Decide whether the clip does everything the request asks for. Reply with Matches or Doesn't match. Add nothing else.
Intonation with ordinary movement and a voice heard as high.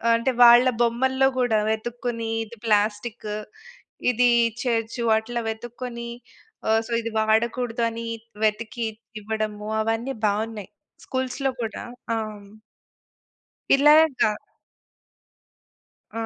Doesn't match